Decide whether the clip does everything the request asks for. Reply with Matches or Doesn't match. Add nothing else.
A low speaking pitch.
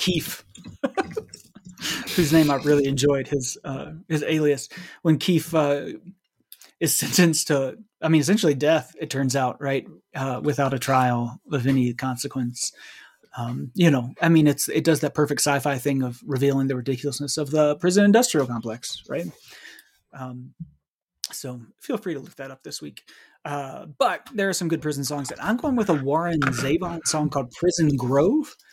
Doesn't match